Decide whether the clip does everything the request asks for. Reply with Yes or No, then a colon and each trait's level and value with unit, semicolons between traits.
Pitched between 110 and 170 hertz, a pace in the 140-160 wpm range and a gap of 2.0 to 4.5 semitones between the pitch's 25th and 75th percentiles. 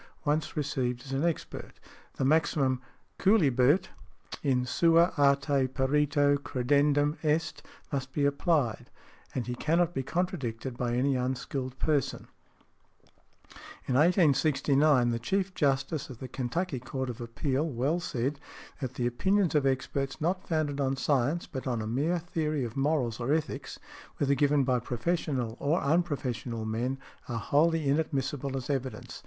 Yes: medium, 140 Hz; average, 145 wpm; average, 3.3 semitones